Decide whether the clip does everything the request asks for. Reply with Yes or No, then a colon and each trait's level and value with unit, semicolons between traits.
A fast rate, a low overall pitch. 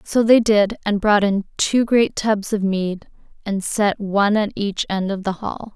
No: fast, 210 wpm; high, 205 Hz